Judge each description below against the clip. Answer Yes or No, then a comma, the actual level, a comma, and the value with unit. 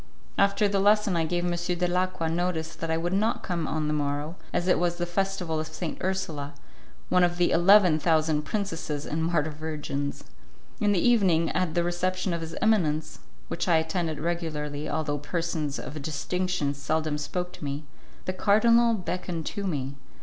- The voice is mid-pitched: Yes, medium, 170 Hz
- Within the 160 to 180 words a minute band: Yes, average, 175 wpm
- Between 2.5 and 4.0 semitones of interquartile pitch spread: Yes, average, 2.9 semitones